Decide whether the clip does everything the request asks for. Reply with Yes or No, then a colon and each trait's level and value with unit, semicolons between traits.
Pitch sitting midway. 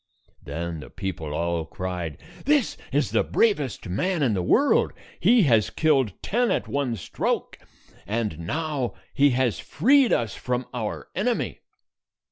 No: low, 125 Hz